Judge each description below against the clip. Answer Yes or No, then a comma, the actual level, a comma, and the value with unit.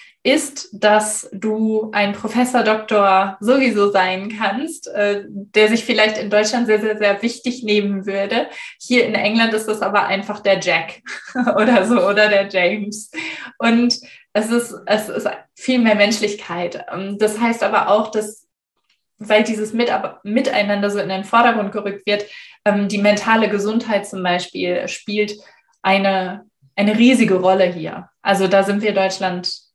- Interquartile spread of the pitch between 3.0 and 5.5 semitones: No, narrow, 2.5 semitones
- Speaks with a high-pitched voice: Yes, high, 210 Hz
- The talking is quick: No, average, 145 wpm